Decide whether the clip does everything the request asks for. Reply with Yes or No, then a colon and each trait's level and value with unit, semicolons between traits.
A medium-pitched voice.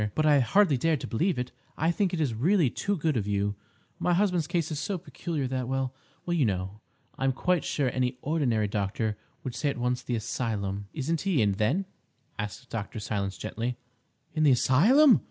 No: low, 130 Hz